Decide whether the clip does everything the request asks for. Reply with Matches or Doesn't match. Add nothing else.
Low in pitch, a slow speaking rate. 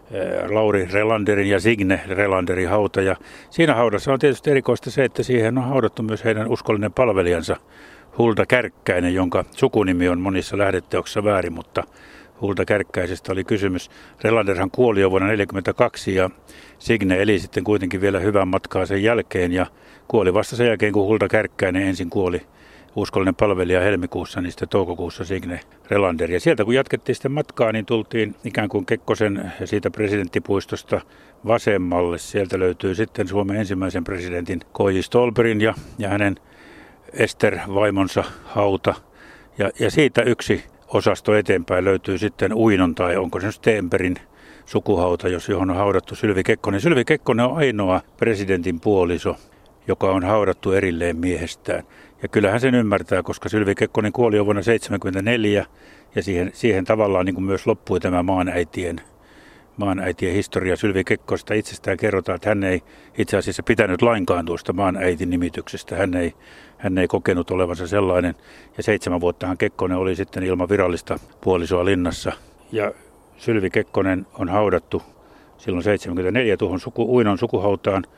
Doesn't match